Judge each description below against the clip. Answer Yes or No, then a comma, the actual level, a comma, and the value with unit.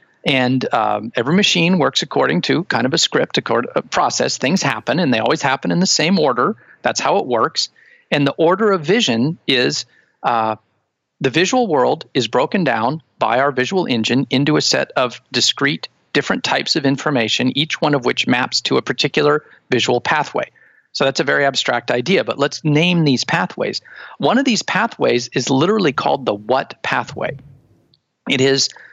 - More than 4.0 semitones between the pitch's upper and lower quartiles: Yes, average, 5.1 semitones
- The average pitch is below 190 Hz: Yes, medium, 140 Hz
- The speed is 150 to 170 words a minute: No, average, 185 wpm